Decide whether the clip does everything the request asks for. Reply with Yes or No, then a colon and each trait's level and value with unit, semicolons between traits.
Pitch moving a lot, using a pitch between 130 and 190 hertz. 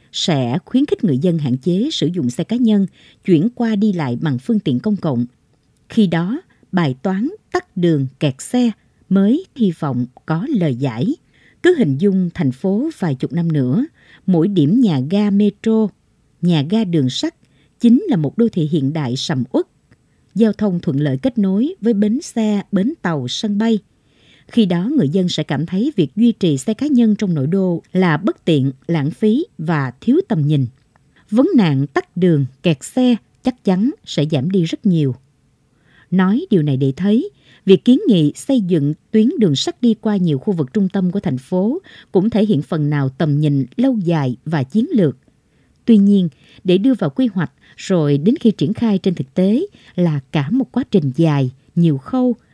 Yes: wide, 7.1 semitones; medium, 185 Hz